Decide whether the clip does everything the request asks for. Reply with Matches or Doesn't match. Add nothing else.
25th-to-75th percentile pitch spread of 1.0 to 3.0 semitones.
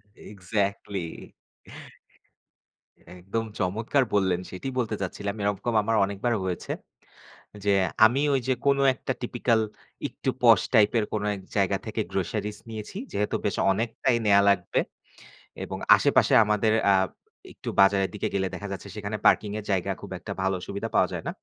Matches